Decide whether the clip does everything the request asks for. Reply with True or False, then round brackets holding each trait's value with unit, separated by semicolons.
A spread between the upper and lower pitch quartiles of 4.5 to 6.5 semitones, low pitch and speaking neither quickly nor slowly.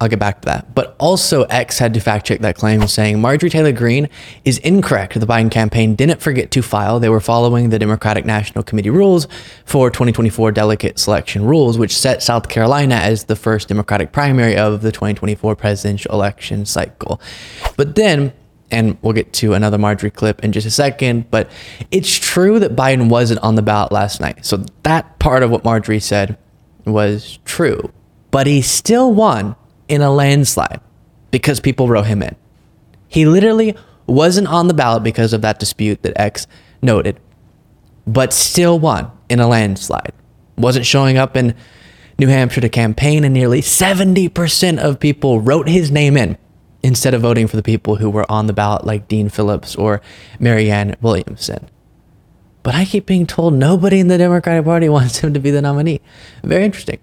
True (5.2 semitones; 120 Hz; 180 wpm)